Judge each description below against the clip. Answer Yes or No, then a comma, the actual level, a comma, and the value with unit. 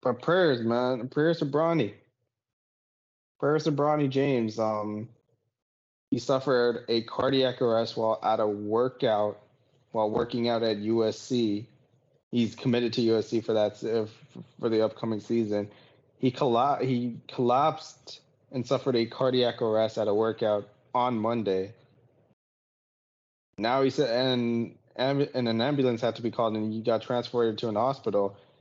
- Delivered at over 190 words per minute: No, average, 145 wpm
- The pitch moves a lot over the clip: No, average, 2.7 semitones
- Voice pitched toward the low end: Yes, low, 115 Hz